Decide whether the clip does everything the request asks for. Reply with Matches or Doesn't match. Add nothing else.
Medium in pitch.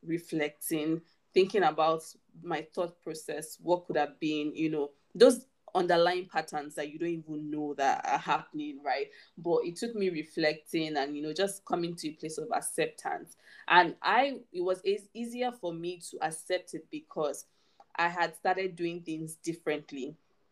Matches